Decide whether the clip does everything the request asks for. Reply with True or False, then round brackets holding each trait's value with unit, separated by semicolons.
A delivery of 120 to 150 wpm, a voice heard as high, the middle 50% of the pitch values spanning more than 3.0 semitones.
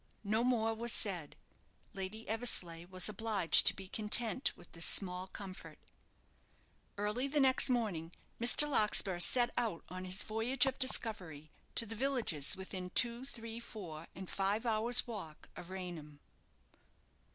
True (140 wpm; 210 Hz; 4.5 semitones)